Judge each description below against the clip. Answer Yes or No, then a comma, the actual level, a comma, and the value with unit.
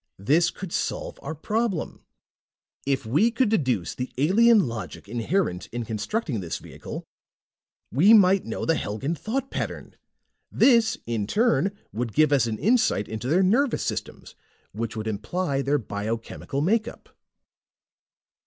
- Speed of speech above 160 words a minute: No, slow, 135 wpm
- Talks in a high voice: No, medium, 145 Hz